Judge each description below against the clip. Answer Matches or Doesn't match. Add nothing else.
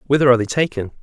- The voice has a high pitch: Doesn't match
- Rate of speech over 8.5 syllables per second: Matches